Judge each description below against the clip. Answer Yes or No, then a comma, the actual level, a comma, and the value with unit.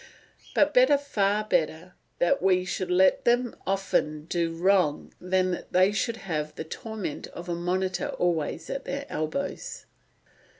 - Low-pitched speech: No, medium, 185 Hz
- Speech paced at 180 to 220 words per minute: No, average, 145 wpm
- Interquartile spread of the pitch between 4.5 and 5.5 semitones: No, average, 3.5 semitones